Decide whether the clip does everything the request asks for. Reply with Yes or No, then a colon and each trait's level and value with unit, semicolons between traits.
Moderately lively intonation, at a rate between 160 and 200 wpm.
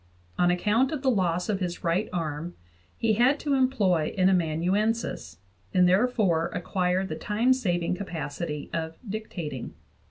No: average, 4.5 semitones; average, 140 wpm